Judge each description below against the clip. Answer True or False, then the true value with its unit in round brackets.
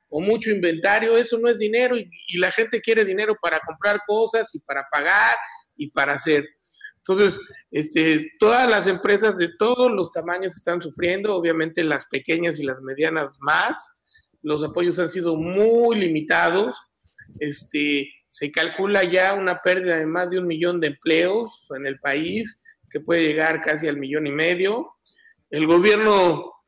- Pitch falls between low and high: True (175 Hz)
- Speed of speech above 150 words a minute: True (160 wpm)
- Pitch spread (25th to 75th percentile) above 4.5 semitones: True (5.1 semitones)